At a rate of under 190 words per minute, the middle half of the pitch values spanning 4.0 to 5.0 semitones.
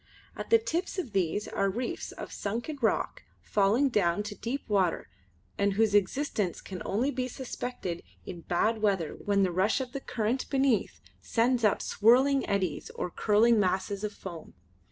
Yes: average, 165 wpm; average, 4.5 semitones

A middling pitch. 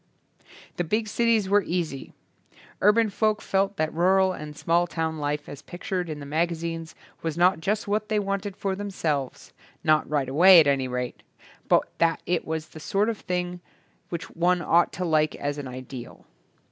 Yes: medium, 170 Hz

